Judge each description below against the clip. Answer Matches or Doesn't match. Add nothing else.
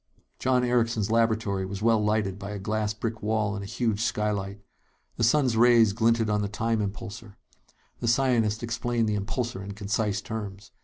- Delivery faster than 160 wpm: Matches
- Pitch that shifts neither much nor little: Doesn't match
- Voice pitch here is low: Matches